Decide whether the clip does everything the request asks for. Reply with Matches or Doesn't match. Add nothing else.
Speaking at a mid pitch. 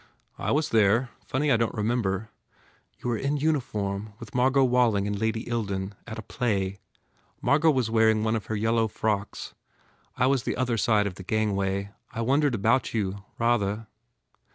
Doesn't match